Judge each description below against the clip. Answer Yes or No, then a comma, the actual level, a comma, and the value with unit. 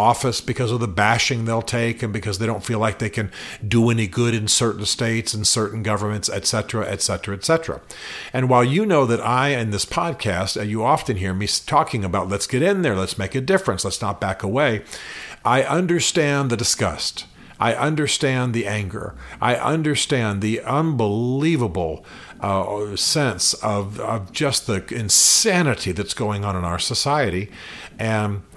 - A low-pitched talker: Yes, low, 115 Hz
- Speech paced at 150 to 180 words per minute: Yes, average, 170 wpm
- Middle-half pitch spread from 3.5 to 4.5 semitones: Yes, average, 4.1 semitones